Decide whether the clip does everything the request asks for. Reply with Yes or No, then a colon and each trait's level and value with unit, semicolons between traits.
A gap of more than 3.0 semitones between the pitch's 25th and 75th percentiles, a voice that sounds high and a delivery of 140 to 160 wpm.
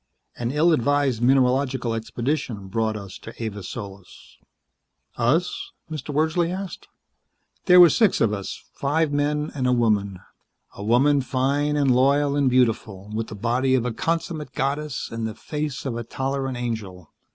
No: average, 4.5 semitones; low, 130 Hz; average, 155 wpm